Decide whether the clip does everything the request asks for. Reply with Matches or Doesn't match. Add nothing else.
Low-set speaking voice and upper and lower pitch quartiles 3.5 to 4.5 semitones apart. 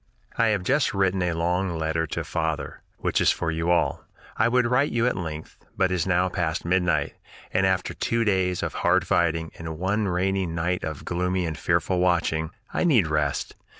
Doesn't match